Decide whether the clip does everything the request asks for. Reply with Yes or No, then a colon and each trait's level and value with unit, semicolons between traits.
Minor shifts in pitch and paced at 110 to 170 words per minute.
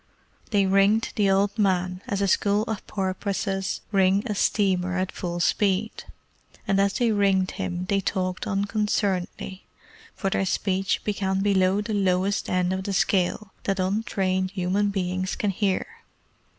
Yes: narrow, 1.5 semitones; average, 150 wpm